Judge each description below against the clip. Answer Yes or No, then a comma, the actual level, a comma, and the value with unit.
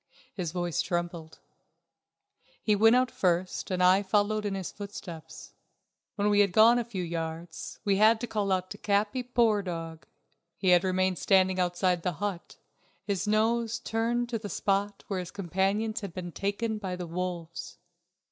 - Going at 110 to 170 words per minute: Yes, average, 165 wpm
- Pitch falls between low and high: No, high, 195 Hz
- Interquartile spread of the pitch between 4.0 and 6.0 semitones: No, average, 3.2 semitones